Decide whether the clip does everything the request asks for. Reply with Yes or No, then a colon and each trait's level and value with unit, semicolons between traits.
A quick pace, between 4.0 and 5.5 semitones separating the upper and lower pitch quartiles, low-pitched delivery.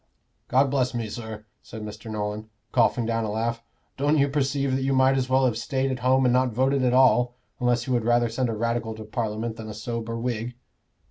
No: fast, 220 wpm; average, 2.7 semitones; low, 120 Hz